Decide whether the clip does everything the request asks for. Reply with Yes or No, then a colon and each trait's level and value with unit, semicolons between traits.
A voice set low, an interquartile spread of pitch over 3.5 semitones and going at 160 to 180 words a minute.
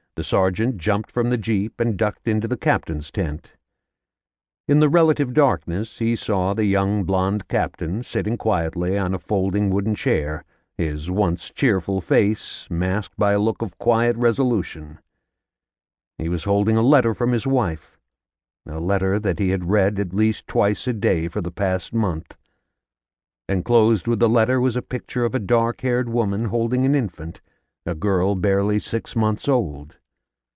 Yes: low, 100 Hz; average, 4.9 semitones; average, 165 wpm